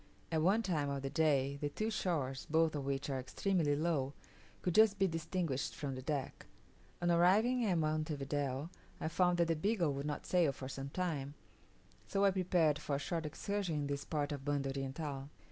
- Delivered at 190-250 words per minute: Yes, average, 195 wpm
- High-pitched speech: No, medium, 155 Hz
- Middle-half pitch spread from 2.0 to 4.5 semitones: Yes, average, 4.1 semitones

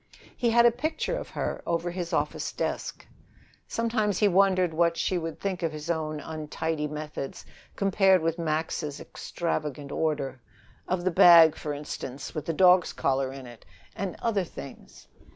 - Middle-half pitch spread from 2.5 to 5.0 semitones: Yes, average, 3.7 semitones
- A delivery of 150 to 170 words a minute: Yes, average, 160 wpm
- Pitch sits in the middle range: Yes, medium, 165 Hz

